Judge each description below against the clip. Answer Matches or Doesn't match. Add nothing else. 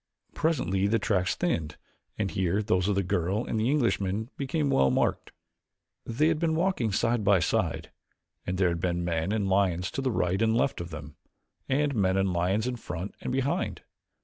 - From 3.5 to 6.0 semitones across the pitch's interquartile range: Matches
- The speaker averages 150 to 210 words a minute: Matches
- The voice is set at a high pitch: Doesn't match